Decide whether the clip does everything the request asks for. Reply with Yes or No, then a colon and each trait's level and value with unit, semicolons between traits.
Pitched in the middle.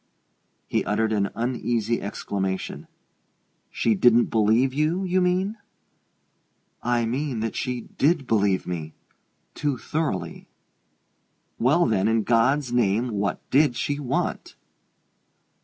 No: low, 120 Hz